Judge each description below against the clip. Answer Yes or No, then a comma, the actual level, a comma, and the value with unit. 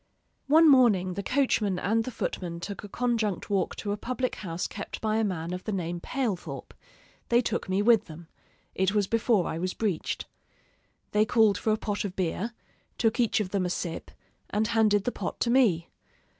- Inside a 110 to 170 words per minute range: No, average, 195 wpm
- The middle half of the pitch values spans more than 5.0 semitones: No, average, 3.7 semitones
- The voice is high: Yes, high, 205 Hz